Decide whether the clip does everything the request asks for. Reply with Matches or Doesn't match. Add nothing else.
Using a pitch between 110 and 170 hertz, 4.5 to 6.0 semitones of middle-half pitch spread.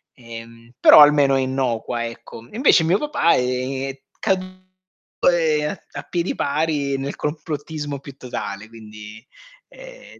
Matches